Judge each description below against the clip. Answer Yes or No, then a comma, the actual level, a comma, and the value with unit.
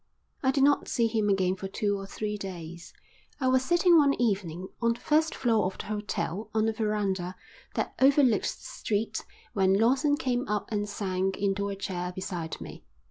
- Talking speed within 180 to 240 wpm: Yes, average, 190 wpm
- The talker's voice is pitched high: Yes, high, 210 Hz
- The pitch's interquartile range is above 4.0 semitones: Yes, average, 4.4 semitones